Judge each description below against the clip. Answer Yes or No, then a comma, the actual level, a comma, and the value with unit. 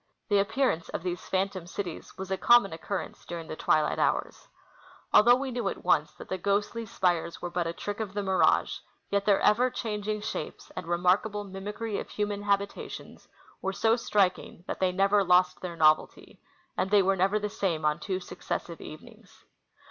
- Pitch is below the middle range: No, high, 195 Hz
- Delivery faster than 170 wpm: Yes, average, 185 wpm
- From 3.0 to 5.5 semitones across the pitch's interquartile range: No, narrow, 2.6 semitones